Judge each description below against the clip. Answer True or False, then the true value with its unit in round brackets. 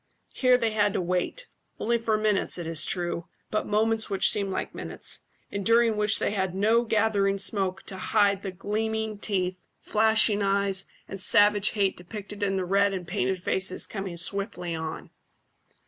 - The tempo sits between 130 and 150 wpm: False (170 wpm)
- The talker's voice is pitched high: True (200 Hz)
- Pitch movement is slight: True (2.2 semitones)